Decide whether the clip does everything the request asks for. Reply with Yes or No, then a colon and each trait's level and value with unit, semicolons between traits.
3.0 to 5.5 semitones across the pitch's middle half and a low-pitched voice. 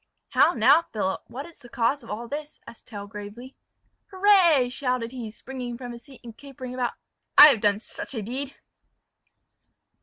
No: average, 3.5 semitones; very high, 250 Hz